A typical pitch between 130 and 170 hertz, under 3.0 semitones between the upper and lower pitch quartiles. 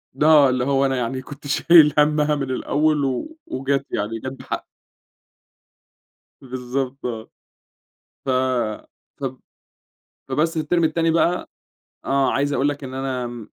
Yes: medium, 140 Hz; narrow, 2.5 semitones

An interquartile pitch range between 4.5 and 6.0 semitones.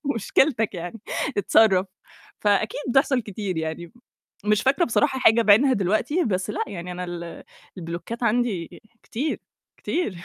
Yes: average, 5.1 semitones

